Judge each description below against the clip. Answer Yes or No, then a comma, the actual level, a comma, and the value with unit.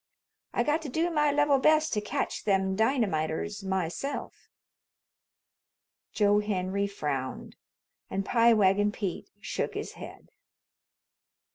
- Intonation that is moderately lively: No, wide, 6.5 semitones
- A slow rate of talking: Yes, slow, 115 wpm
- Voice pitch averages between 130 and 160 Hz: No, high, 205 Hz